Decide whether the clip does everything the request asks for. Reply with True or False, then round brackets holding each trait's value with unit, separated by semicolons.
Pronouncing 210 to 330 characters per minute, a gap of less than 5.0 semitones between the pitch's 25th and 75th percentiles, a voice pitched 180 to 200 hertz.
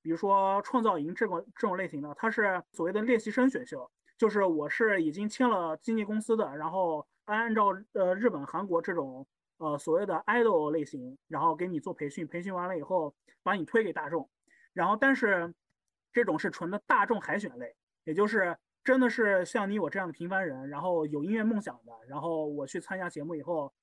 False (310 characters per minute; 5.4 semitones; 185 Hz)